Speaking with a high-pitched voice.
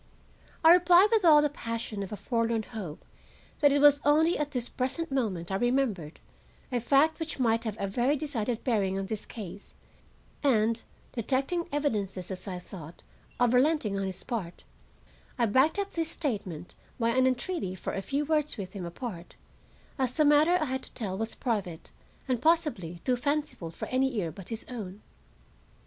Yes: high, 240 Hz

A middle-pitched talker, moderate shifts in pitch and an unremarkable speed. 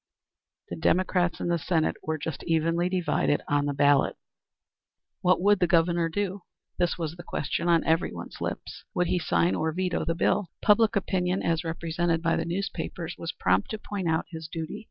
No: medium, 170 Hz; narrow, 2.1 semitones; average, 180 wpm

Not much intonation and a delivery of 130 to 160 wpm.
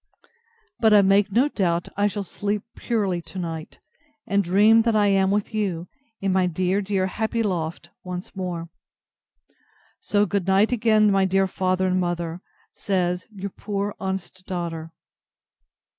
Yes: narrow, 2.3 semitones; average, 150 wpm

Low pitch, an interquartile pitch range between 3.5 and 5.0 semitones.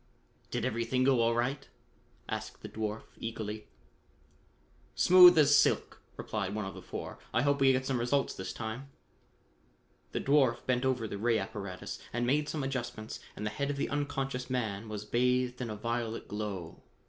Yes: low, 120 Hz; average, 3.8 semitones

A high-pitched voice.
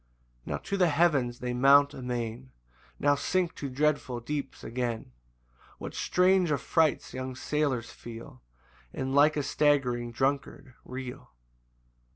No: low, 135 Hz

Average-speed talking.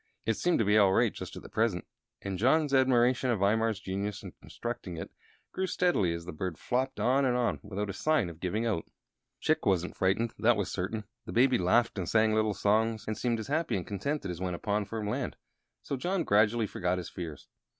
No: fast, 210 wpm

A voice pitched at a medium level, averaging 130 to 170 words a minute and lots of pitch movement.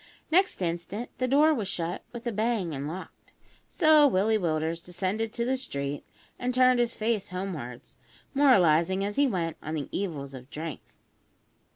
No: high, 195 Hz; average, 165 wpm; wide, 6.7 semitones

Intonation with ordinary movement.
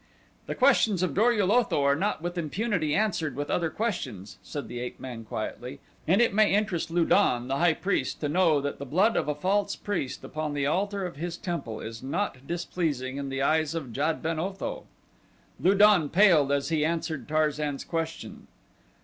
Yes: average, 5.0 semitones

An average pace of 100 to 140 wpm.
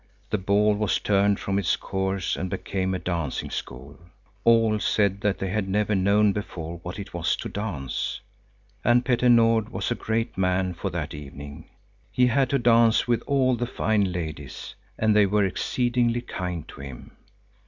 No: average, 175 wpm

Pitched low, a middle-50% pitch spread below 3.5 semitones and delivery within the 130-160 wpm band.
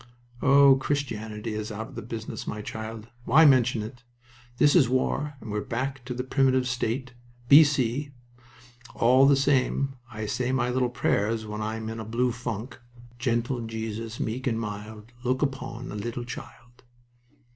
Yes: low, 120 Hz; average, 2.9 semitones; average, 155 wpm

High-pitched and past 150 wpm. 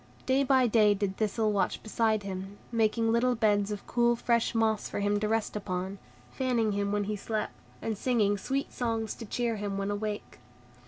Yes: high, 215 Hz; average, 190 wpm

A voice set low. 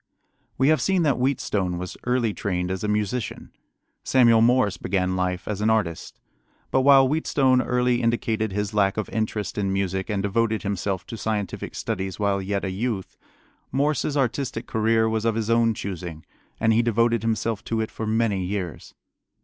Yes: low, 110 Hz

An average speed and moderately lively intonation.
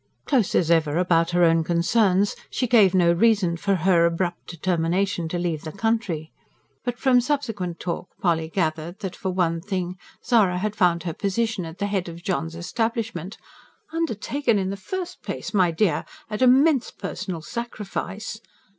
Yes: average, 165 wpm; average, 4.4 semitones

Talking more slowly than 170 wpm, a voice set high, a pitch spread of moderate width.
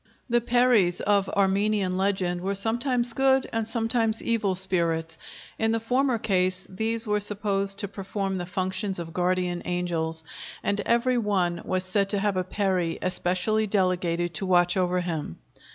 Yes: average, 155 wpm; high, 195 Hz; average, 3.4 semitones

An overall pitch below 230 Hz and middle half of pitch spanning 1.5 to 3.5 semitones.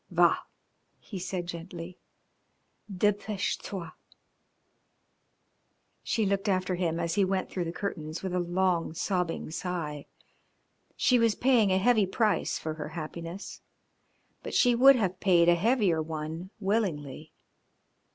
Yes: medium, 185 Hz; average, 3.2 semitones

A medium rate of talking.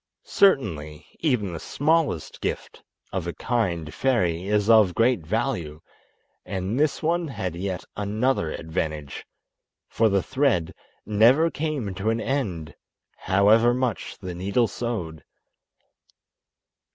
No: slow, 115 wpm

